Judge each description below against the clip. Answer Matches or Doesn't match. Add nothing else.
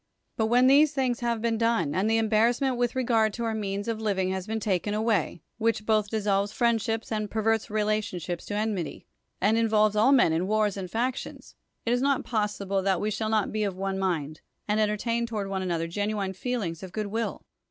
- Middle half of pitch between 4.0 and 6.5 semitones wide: Doesn't match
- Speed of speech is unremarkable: Doesn't match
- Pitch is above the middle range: Matches